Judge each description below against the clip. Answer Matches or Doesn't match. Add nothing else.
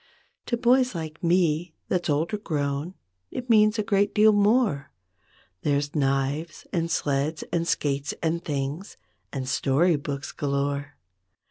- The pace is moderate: Doesn't match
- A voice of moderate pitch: Matches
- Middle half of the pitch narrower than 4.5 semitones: Doesn't match